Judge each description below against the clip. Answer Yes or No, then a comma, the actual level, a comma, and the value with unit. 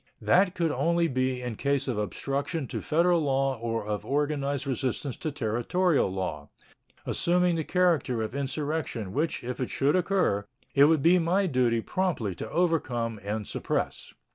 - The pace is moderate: Yes, average, 160 wpm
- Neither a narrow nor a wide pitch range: No, wide, 5.8 semitones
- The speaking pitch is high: No, medium, 140 Hz